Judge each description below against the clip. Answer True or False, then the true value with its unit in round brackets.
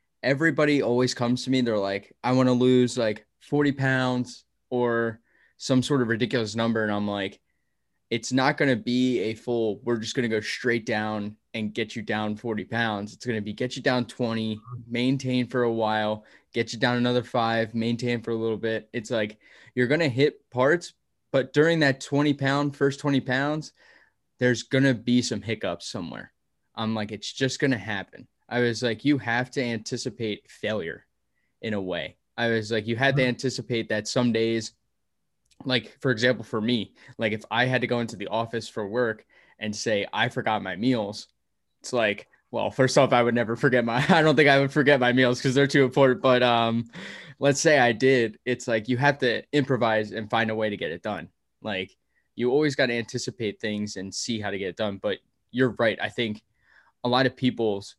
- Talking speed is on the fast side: True (210 wpm)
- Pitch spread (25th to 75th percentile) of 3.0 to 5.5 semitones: False (2.6 semitones)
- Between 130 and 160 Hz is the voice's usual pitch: False (120 Hz)